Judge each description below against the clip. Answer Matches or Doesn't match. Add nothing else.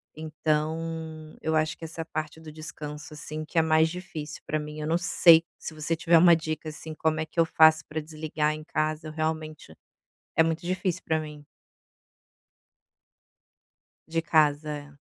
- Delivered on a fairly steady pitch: Matches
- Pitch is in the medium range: Matches